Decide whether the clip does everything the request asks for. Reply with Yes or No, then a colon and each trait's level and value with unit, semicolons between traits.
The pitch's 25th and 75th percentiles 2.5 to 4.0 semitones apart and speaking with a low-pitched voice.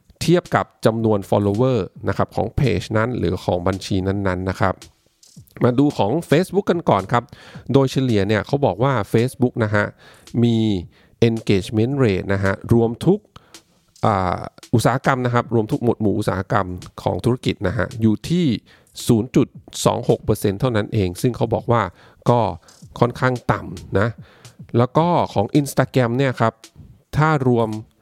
No: average, 4.5 semitones; low, 115 Hz